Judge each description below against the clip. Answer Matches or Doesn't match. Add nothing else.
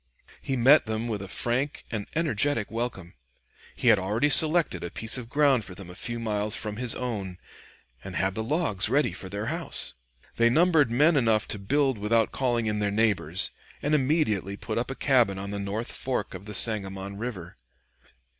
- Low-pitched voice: Matches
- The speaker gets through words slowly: Doesn't match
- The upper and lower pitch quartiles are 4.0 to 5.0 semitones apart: Matches